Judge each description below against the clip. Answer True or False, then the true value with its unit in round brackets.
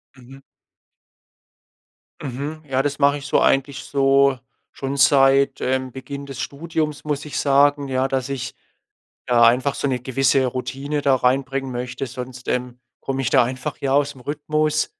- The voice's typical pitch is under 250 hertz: True (135 Hz)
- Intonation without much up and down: True (1.7 semitones)